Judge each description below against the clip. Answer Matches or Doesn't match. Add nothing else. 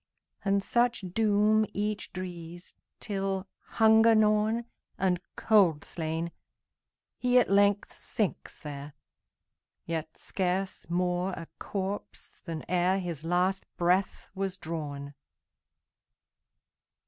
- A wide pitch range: Doesn't match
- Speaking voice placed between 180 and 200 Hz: Matches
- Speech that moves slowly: Matches